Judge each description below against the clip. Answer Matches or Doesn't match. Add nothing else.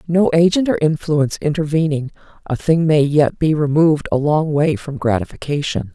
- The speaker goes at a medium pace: Matches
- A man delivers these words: Doesn't match